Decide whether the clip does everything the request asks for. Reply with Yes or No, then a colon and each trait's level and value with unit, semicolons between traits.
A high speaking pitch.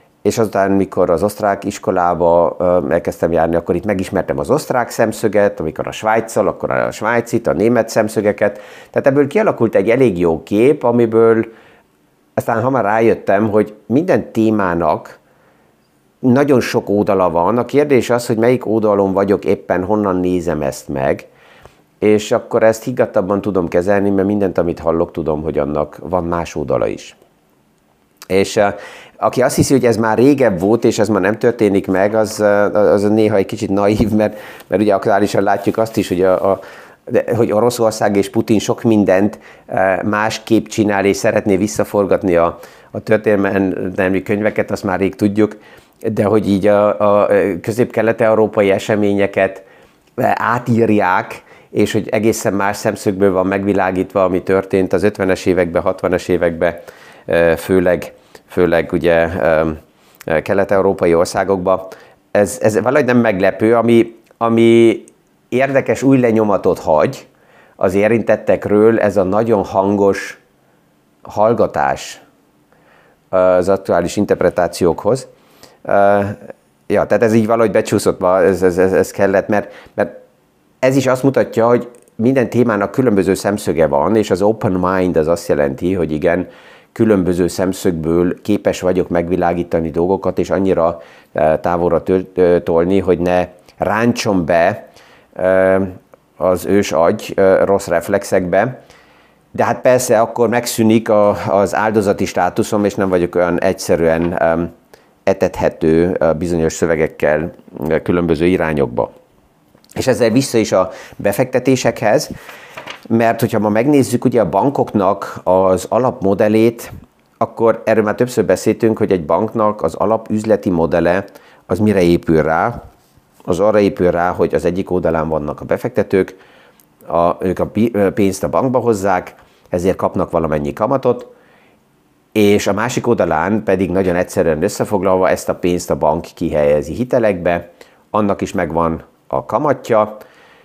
No: low, 100 Hz